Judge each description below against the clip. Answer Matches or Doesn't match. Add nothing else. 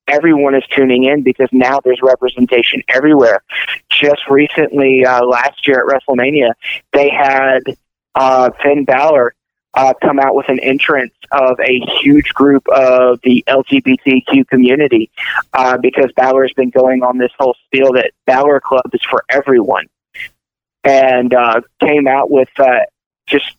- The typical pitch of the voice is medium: Doesn't match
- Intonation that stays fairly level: Matches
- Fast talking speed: Doesn't match